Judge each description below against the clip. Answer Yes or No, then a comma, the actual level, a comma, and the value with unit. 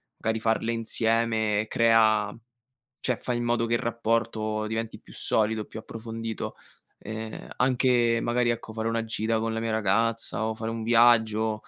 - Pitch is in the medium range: No, low, 115 Hz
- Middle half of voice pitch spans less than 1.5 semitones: Yes, narrow, 0.9 semitones